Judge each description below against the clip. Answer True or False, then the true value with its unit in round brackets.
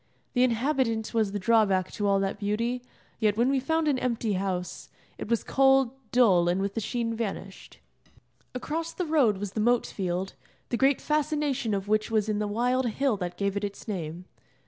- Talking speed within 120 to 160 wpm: False (190 wpm)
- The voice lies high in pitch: True (225 Hz)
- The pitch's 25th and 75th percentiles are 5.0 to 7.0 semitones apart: False (4.3 semitones)